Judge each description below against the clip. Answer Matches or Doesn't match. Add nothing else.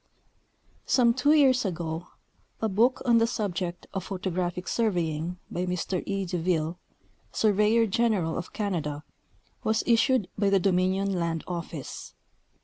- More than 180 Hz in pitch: Matches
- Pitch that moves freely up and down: Doesn't match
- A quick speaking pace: Doesn't match